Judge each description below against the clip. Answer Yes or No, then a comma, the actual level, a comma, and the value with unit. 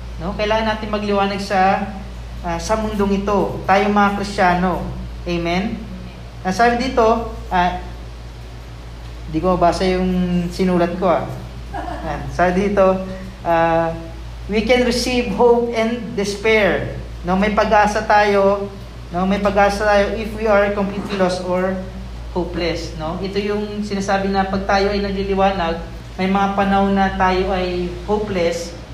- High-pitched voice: Yes, high, 195 Hz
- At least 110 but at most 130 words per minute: No, average, 140 wpm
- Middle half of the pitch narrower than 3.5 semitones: Yes, average, 2.9 semitones